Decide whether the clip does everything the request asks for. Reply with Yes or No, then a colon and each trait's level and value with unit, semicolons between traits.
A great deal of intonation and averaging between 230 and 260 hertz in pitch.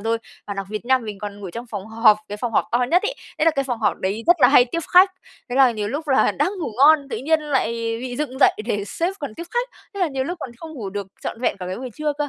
Yes: wide, 6.1 semitones; very high, 255 Hz